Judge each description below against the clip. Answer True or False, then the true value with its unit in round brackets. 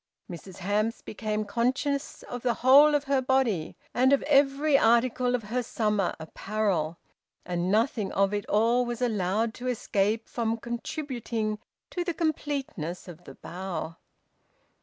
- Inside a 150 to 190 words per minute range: False (140 wpm)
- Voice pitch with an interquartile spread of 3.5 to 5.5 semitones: True (4.4 semitones)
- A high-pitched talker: True (230 Hz)